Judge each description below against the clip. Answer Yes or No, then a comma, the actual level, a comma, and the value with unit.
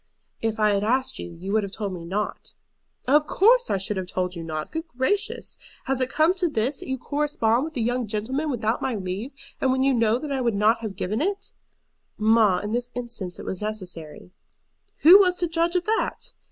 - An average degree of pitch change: No, wide, 6.3 semitones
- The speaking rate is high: Yes, fast, 220 wpm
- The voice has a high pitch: Yes, high, 235 Hz